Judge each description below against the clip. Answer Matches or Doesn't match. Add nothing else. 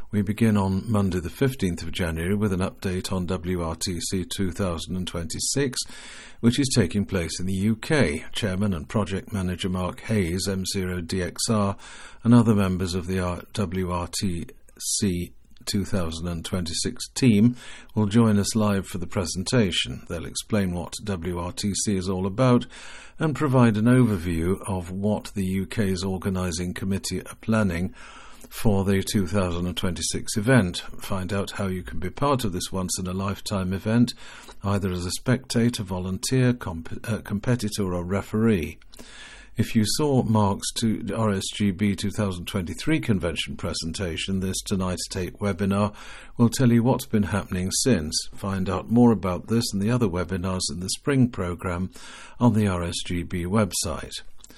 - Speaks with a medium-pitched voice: Doesn't match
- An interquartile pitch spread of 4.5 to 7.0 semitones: Doesn't match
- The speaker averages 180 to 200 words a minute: Doesn't match